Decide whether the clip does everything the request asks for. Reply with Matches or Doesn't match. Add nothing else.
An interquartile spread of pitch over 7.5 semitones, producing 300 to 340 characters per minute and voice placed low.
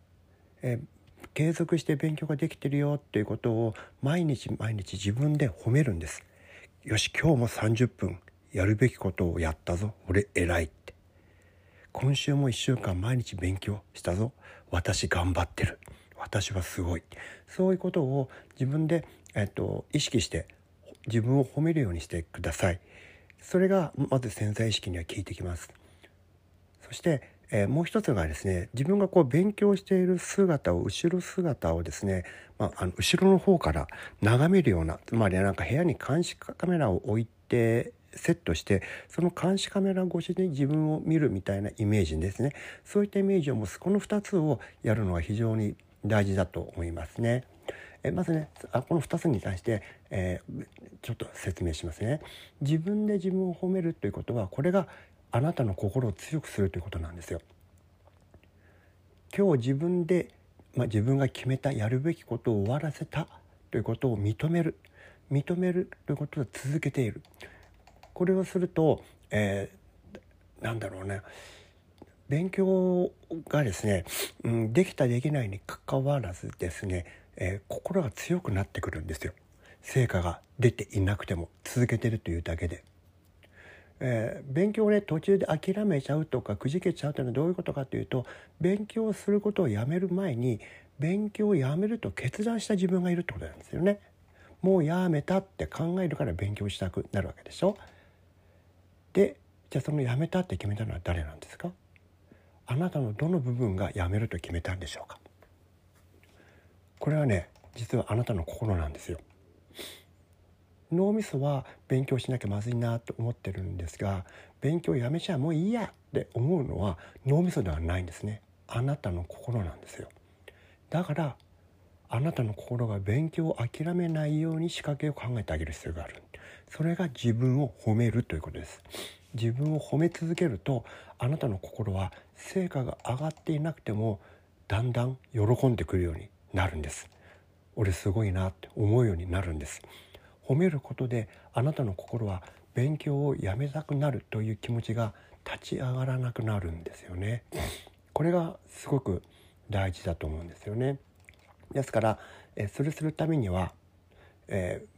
Matches